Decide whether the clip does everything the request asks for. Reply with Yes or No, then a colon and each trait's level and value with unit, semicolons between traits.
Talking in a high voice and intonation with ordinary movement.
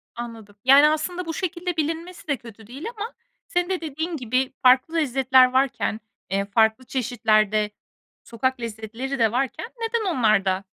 No: very high, 260 Hz; wide, 6.2 semitones